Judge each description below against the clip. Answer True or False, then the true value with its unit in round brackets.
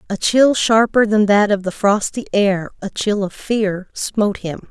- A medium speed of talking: True (165 wpm)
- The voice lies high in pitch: True (205 Hz)